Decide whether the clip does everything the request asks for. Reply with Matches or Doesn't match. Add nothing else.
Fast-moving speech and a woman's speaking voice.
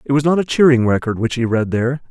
Doesn't match